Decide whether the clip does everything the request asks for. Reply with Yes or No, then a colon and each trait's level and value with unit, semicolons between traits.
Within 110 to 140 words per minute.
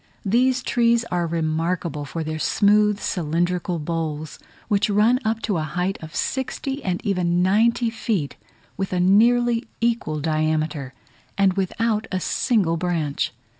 Yes: slow, 135 wpm